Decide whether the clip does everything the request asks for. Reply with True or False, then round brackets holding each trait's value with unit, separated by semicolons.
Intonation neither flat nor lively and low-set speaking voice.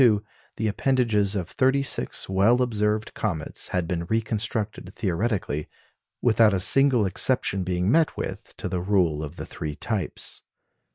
True (4.1 semitones; 105 Hz)